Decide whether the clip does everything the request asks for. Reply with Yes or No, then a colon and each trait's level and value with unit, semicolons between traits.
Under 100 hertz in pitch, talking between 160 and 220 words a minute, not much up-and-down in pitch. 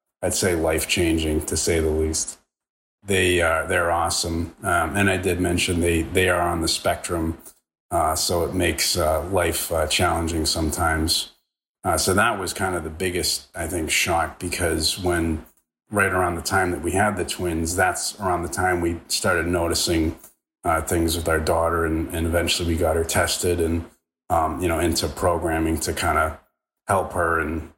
Yes: very low, 85 Hz; average, 180 wpm; narrow, 1.5 semitones